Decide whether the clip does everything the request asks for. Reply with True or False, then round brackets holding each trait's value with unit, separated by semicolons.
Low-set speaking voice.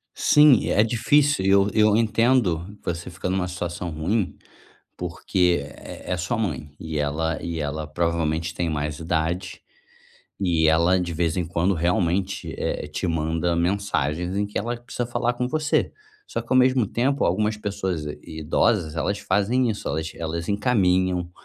True (90 Hz)